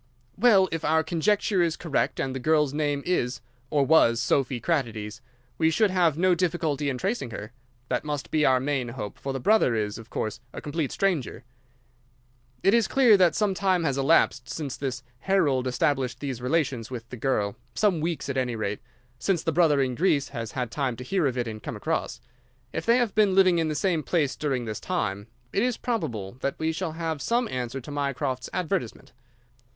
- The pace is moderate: Yes, average, 195 wpm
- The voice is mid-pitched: Yes, medium, 145 Hz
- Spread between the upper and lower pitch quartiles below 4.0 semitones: No, wide, 5.6 semitones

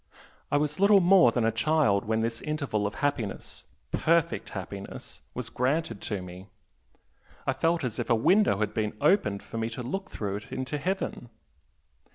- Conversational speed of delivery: Yes, average, 175 wpm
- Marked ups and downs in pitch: Yes, wide, 6.9 semitones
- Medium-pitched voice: No, low, 120 Hz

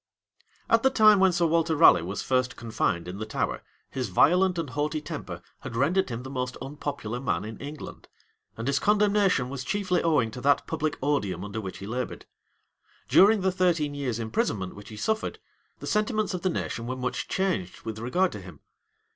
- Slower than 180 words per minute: No, average, 195 wpm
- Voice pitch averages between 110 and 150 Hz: Yes, medium, 140 Hz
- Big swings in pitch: Yes, wide, 8.0 semitones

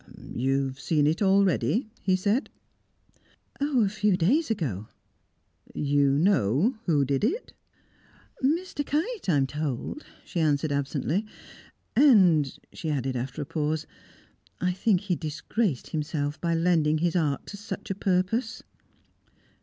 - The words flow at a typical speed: No, slow, 130 wpm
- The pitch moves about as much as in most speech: No, wide, 6.3 semitones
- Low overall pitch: No, medium, 170 Hz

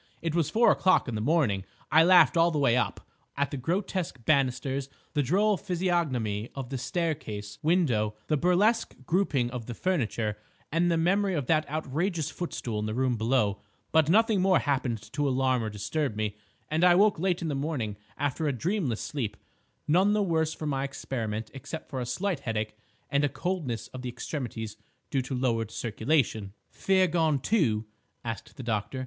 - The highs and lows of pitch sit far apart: Yes, wide, 6.2 semitones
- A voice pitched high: No, medium, 140 Hz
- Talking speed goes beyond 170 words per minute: Yes, average, 180 wpm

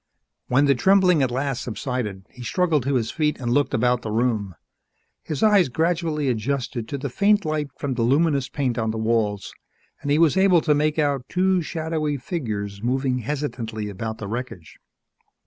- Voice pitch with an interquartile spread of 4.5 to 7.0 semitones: Yes, average, 4.9 semitones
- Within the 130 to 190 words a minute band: Yes, average, 180 wpm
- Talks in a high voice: No, low, 135 Hz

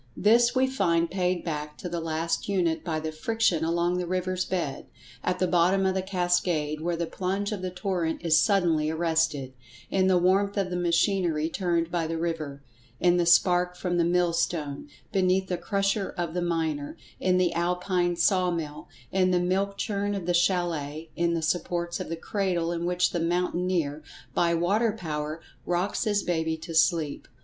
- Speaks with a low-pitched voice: No, medium, 175 Hz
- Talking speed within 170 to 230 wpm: Yes, average, 180 wpm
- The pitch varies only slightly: Yes, narrow, 2.0 semitones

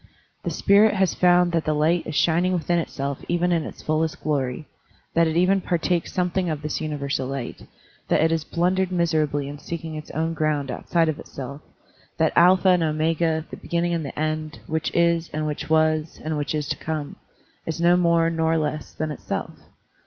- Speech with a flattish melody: Yes, narrow, 2.0 semitones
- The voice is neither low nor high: Yes, medium, 160 Hz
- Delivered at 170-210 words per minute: Yes, average, 190 wpm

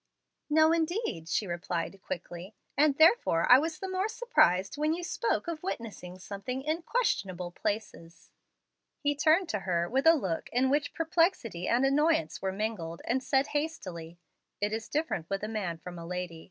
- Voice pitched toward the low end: No, high, 230 Hz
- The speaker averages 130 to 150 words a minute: No, average, 170 wpm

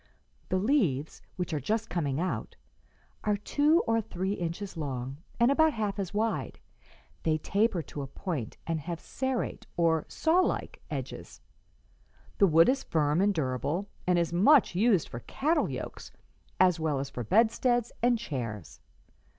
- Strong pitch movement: Yes, wide, 6.6 semitones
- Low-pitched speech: No, medium, 185 Hz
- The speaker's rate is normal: Yes, average, 150 wpm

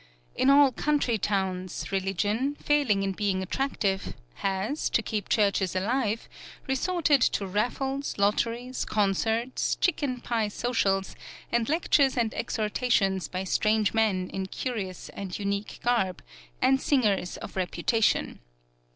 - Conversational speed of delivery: No, slow, 120 wpm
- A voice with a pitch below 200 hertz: No, high, 215 Hz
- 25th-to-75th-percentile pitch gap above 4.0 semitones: Yes, average, 4.7 semitones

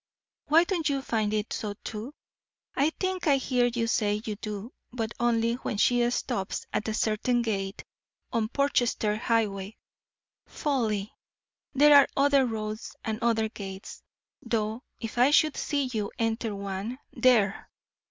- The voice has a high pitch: Yes, high, 230 Hz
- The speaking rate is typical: Yes, average, 145 wpm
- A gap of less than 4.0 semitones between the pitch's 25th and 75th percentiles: Yes, average, 3.2 semitones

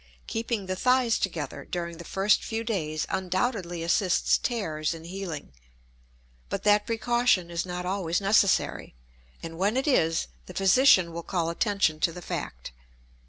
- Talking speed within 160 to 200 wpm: No, average, 150 wpm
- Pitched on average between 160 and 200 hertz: Yes, medium, 185 Hz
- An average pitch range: Yes, average, 4.1 semitones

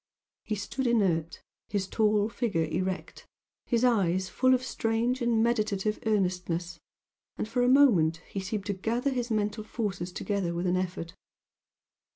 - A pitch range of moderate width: Yes, average, 4.3 semitones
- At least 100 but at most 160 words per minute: Yes, average, 150 wpm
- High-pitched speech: Yes, high, 210 Hz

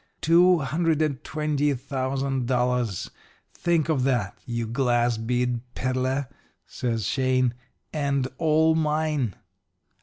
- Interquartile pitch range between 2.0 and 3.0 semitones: No, average, 3.6 semitones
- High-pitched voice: No, low, 135 Hz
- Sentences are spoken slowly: Yes, slow, 110 wpm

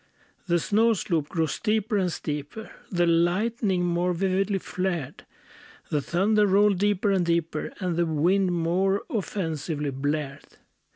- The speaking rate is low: Yes, slow, 130 wpm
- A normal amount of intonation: Yes, average, 3.3 semitones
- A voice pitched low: No, medium, 180 Hz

